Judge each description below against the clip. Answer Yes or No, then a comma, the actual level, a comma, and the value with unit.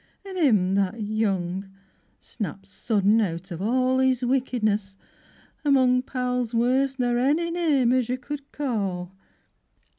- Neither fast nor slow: No, slow, 130 wpm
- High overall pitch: Yes, high, 245 Hz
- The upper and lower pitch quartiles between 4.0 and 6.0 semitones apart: Yes, average, 4.7 semitones